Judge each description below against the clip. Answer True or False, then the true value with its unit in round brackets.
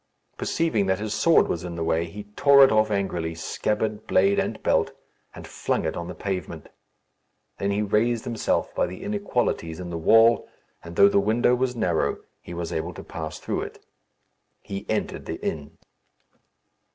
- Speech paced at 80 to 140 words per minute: False (175 wpm)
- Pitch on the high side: False (100 Hz)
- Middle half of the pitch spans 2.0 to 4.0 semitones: False (4.7 semitones)